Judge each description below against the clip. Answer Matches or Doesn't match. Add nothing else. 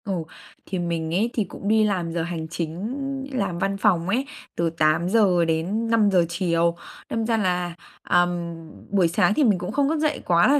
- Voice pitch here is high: Doesn't match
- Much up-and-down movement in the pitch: Doesn't match